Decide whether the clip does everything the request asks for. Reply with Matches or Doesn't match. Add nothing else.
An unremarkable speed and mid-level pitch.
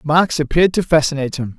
Matches